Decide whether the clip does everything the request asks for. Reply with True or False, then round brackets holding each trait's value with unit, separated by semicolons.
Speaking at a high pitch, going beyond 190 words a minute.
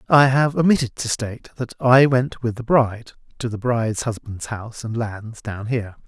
False (120 Hz; 200 wpm)